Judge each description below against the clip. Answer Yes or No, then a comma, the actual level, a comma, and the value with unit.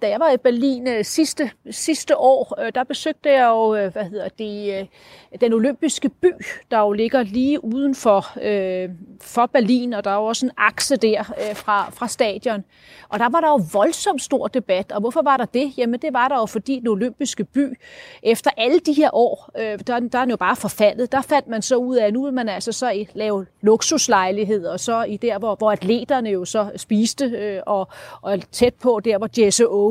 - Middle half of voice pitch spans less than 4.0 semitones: No, average, 4.3 semitones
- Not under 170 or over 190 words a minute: No, average, 220 wpm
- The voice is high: Yes, high, 235 Hz